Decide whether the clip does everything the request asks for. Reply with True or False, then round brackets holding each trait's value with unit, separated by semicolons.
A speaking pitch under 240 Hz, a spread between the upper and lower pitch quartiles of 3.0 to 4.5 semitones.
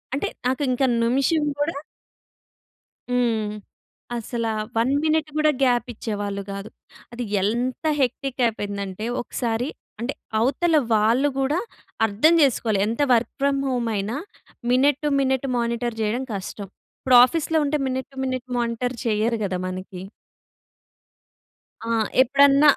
False (245 Hz; 3.6 semitones)